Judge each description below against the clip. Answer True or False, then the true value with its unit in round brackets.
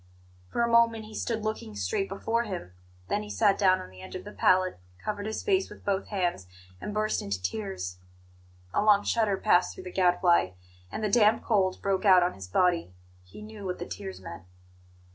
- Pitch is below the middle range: False (190 Hz)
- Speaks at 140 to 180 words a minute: False (200 wpm)